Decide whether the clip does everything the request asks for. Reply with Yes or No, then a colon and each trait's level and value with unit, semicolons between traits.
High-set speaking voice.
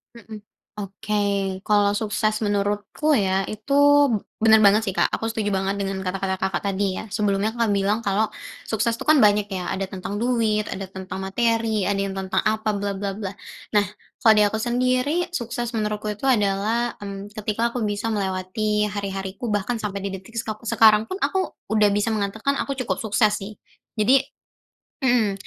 Yes: high, 210 Hz